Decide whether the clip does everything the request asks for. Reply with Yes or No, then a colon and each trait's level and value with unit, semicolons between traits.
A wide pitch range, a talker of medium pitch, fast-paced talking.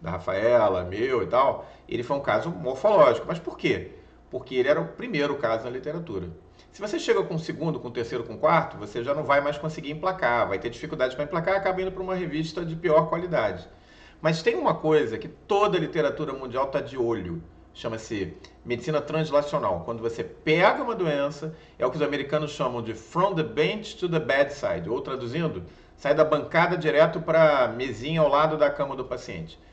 No: average, 4.2 semitones; medium, 150 Hz; fast, 205 wpm